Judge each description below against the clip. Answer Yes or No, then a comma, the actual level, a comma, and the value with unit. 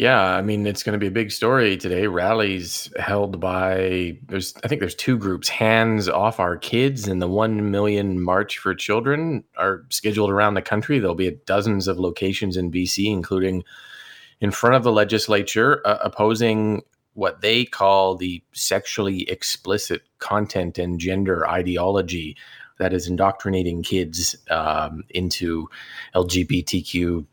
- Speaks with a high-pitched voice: No, very low, 95 Hz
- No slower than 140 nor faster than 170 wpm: Yes, average, 150 wpm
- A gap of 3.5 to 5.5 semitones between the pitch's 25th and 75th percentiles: No, average, 2.7 semitones